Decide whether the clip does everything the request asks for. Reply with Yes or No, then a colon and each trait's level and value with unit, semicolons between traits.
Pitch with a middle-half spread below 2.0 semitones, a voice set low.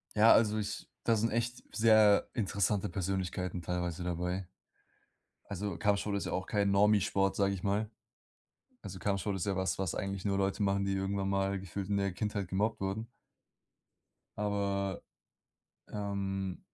Yes: narrow, 1.3 semitones; low, 100 Hz